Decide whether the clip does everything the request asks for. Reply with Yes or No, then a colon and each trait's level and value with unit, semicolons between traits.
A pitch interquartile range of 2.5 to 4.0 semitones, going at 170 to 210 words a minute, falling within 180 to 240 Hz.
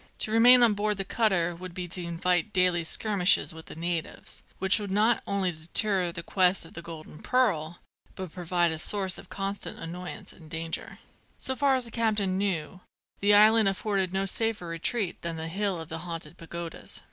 Yes: average, 3.5 semitones; average, 190 wpm; medium, 185 Hz